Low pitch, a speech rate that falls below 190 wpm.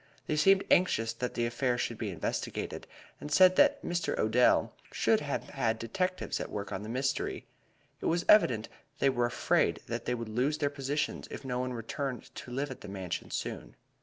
No: low, 125 Hz; average, 195 wpm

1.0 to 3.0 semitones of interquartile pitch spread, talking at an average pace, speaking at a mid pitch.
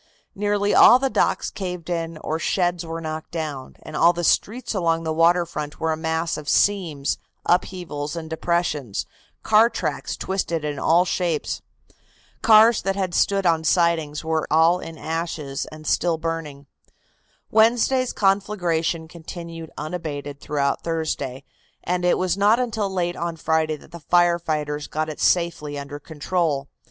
Yes: narrow, 2.5 semitones; average, 155 wpm; medium, 165 Hz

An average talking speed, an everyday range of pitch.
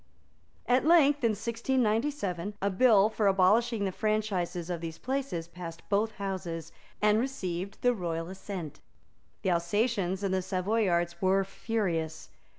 No: slow, 130 wpm; average, 4.3 semitones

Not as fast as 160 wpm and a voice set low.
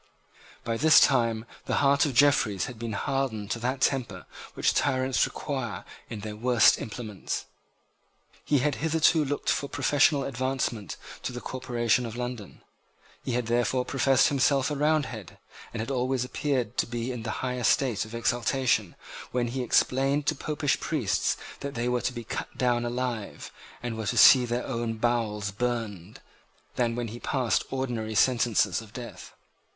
No: average, 165 wpm; low, 125 Hz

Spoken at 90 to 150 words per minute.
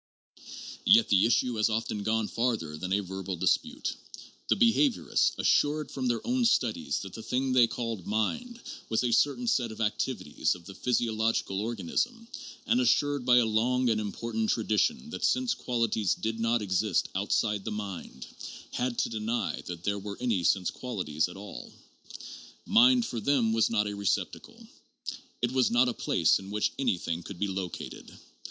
No: average, 175 wpm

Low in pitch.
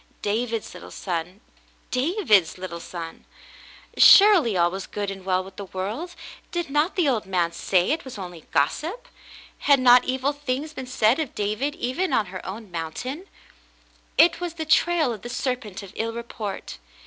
No: high, 230 Hz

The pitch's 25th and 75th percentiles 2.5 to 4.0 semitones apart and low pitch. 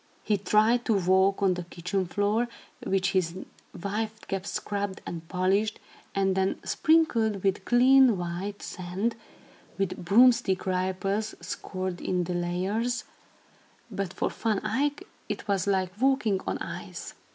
No: average, 2.9 semitones; high, 195 Hz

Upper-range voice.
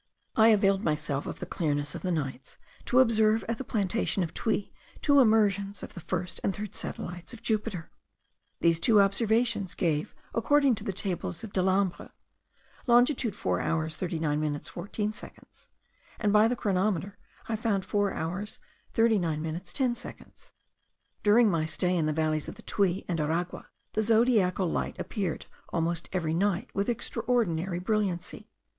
Yes: high, 195 Hz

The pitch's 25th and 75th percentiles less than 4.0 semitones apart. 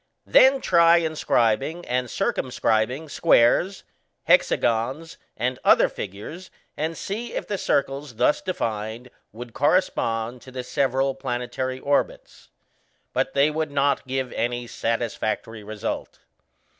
No: average, 5.0 semitones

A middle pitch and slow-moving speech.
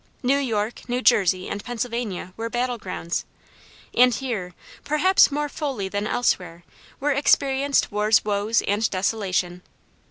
No: high, 225 Hz; slow, 130 wpm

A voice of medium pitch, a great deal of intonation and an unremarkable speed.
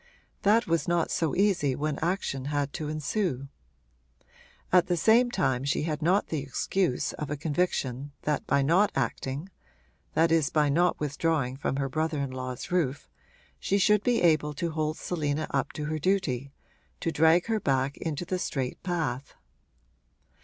No: medium, 155 Hz; average, 4.0 semitones; average, 165 wpm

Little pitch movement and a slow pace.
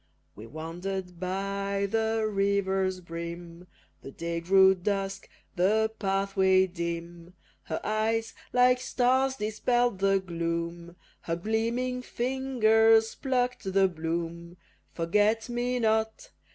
No: average, 4.4 semitones; slow, 105 wpm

